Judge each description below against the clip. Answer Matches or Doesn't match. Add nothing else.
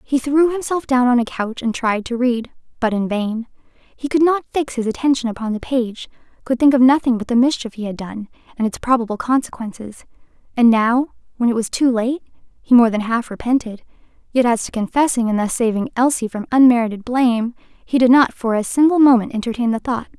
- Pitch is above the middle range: Matches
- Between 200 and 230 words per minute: Matches